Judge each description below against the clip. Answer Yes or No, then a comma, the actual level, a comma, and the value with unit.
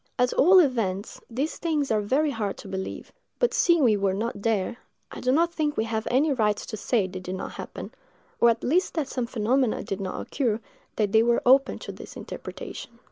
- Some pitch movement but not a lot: Yes, average, 4.9 semitones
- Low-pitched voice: No, high, 235 Hz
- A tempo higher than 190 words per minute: Yes, fast, 205 wpm